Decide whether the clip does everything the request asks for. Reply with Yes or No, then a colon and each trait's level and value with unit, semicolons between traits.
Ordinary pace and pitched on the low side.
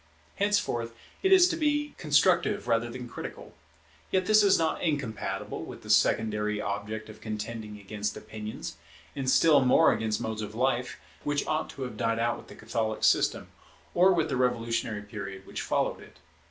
Yes: average, 170 wpm; low, 120 Hz